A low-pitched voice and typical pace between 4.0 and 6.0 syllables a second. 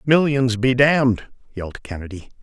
Yes: low, 120 Hz; 5.0 syllables/s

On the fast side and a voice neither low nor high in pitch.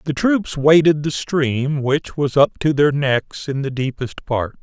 No: average, 195 wpm; medium, 145 Hz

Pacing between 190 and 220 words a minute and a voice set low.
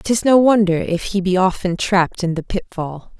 No: fast, 205 wpm; high, 190 Hz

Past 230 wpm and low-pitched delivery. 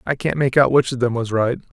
Yes: fast, 300 wpm; low, 125 Hz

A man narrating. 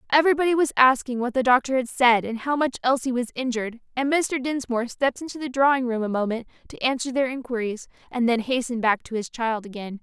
No: female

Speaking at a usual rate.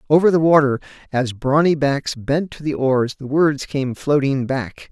Yes: average, 185 wpm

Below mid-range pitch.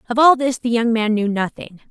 No: high, 235 Hz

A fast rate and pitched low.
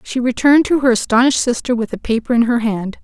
No: fast, 240 wpm; high, 240 Hz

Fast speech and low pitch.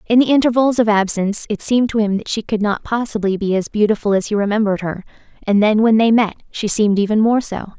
No: fast, 240 wpm; high, 215 Hz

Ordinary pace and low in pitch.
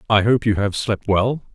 No: fast, 235 wpm; low, 105 Hz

